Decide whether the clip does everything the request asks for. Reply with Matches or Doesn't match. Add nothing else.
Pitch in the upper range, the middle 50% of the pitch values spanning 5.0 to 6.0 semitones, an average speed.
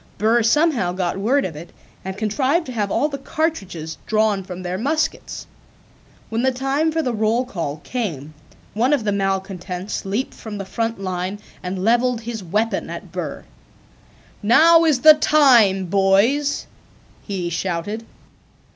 Matches